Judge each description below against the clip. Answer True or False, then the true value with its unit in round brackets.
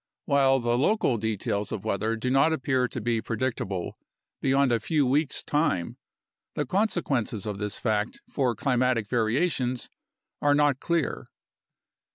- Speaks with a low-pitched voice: True (125 Hz)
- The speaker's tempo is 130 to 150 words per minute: True (140 wpm)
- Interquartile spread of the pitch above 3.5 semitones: True (4.2 semitones)